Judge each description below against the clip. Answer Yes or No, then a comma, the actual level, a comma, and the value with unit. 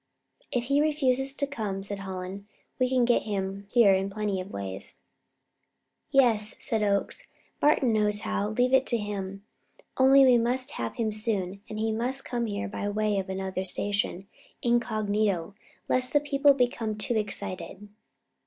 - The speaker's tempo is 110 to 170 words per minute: Yes, average, 160 wpm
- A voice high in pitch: Yes, high, 215 Hz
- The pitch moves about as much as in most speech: Yes, average, 4.0 semitones